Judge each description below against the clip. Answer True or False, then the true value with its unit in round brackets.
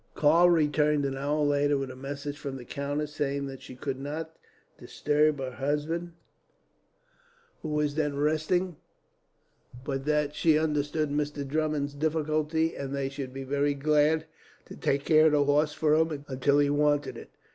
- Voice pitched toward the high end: False (145 Hz)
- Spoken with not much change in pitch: True (1.5 semitones)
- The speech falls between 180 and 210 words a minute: False (165 wpm)